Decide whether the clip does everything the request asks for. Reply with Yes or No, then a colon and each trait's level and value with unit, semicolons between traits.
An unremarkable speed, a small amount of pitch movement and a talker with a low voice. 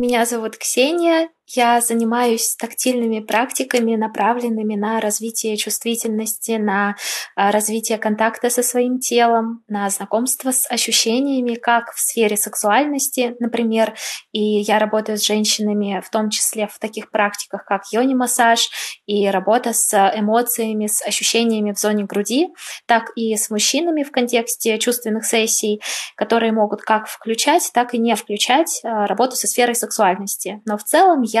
No: average, 140 wpm; narrow, 2.1 semitones; high, 225 Hz